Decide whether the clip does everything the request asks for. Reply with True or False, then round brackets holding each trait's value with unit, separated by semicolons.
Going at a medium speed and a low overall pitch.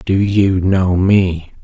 True (145 wpm; 95 Hz)